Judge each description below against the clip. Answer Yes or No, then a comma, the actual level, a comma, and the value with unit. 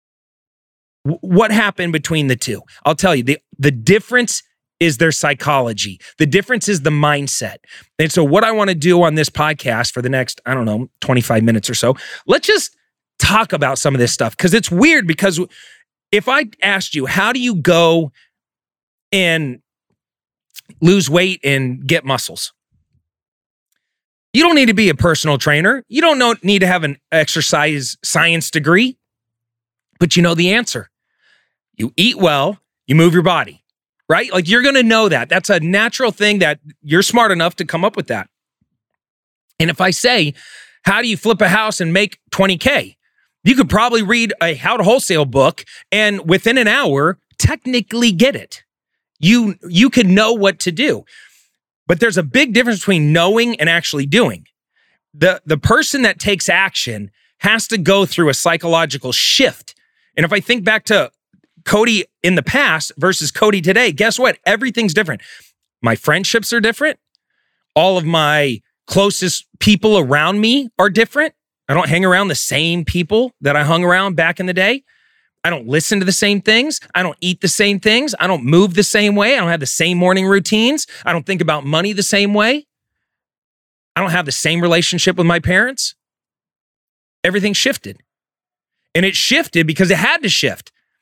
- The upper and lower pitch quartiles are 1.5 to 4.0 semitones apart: No, wide, 5.6 semitones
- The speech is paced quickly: No, average, 180 wpm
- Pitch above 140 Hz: Yes, medium, 185 Hz